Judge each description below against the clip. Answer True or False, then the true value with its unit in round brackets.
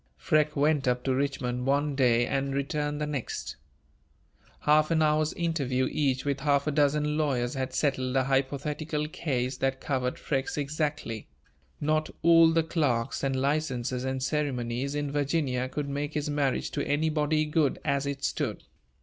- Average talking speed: True (160 wpm)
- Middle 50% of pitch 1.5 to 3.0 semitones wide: True (2.4 semitones)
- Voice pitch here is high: False (140 Hz)